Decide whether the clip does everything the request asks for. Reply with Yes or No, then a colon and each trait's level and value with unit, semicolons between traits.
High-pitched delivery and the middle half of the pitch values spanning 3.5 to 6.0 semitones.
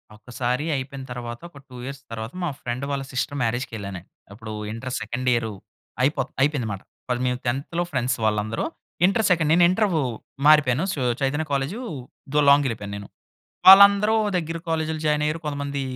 No: low, 135 Hz; average, 4.3 semitones